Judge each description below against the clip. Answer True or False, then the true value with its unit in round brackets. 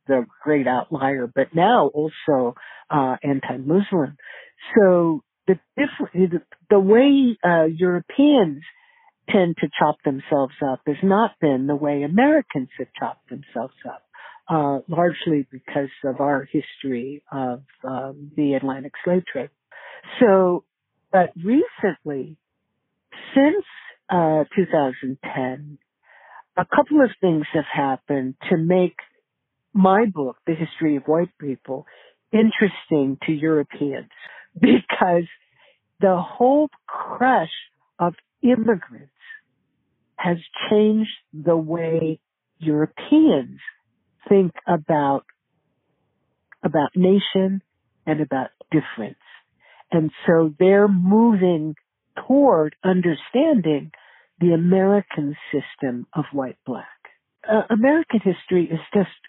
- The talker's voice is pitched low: False (165 Hz)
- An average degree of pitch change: False (5.9 semitones)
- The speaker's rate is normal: False (100 wpm)